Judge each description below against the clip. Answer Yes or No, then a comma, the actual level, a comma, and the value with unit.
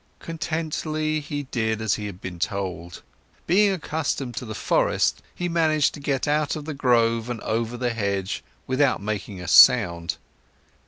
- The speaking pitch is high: No, low, 125 Hz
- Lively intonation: Yes, wide, 6.5 semitones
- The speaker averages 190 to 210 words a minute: No, average, 160 wpm